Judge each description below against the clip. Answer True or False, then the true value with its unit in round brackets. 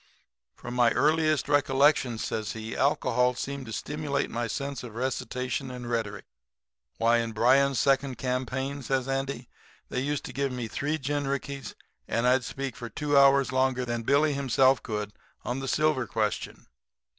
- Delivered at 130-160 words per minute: True (155 wpm)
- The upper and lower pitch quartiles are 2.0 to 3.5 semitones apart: True (2.5 semitones)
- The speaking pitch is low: True (130 Hz)